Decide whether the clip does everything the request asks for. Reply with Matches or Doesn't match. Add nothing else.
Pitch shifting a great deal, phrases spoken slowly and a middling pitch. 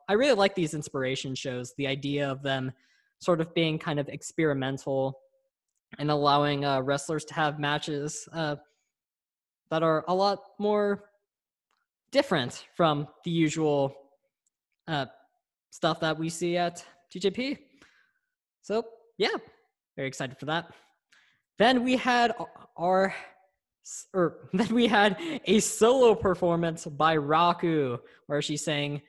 Matches